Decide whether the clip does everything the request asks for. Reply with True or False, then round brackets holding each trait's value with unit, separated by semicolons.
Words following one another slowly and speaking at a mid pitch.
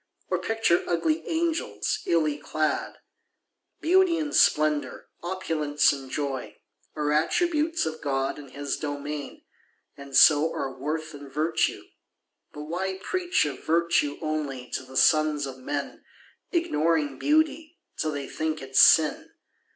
True (130 wpm; 155 Hz)